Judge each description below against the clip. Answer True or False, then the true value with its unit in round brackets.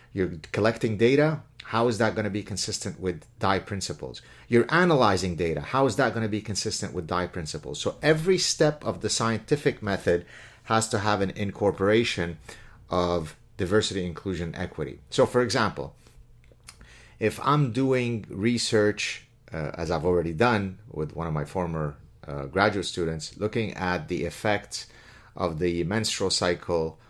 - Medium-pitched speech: False (105 Hz)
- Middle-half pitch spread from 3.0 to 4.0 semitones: False (4.8 semitones)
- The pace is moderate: True (155 wpm)